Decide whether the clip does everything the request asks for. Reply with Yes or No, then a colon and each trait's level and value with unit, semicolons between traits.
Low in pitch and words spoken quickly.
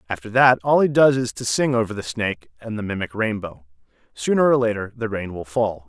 Yes: low, 110 Hz; fast, 225 wpm